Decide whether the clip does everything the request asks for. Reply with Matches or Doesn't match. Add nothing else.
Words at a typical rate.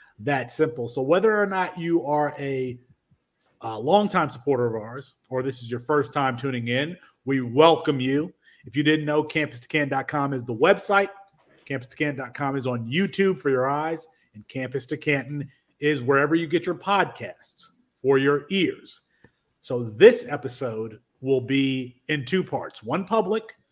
Matches